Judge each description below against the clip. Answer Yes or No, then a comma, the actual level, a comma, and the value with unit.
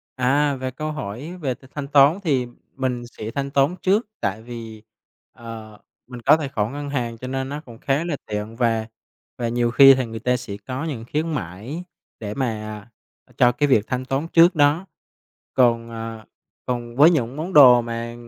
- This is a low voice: Yes, low, 125 Hz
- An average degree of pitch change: Yes, average, 3.8 semitones